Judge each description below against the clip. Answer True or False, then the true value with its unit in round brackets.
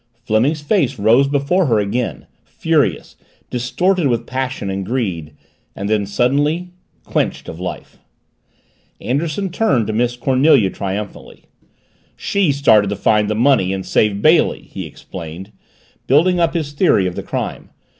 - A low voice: True (125 Hz)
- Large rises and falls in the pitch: True (6.3 semitones)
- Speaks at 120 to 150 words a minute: True (135 wpm)